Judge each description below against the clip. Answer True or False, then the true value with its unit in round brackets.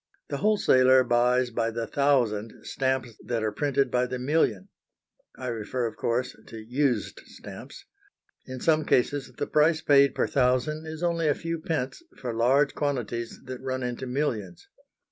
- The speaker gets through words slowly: False (160 wpm)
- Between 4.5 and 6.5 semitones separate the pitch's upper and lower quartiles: False (3.3 semitones)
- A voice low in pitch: True (130 Hz)